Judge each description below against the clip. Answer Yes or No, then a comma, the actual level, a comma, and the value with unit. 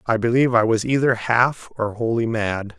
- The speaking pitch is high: No, low, 115 Hz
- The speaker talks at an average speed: Yes, average, 195 wpm